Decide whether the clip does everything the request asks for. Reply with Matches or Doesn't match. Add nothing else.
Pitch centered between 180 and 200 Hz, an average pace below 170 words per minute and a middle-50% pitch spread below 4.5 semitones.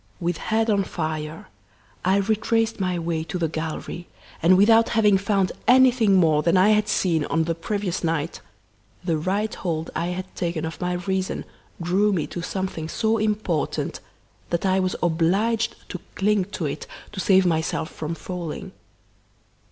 Matches